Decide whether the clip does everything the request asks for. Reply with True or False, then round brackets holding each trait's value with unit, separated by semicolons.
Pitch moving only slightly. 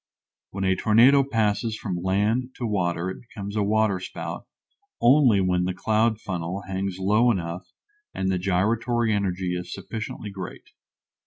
False (3.2 semitones)